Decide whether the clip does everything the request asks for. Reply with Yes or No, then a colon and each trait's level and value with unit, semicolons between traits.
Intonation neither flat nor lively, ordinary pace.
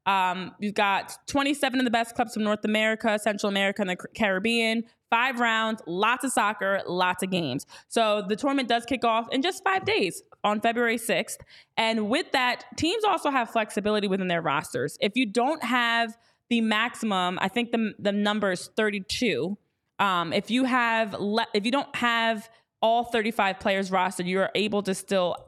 Yes: average, 3.3 semitones; average, 185 wpm